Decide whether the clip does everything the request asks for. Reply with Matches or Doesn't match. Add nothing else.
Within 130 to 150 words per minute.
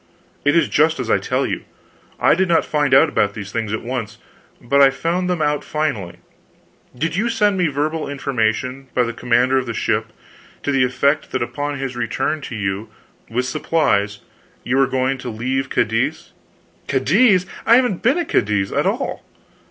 Doesn't match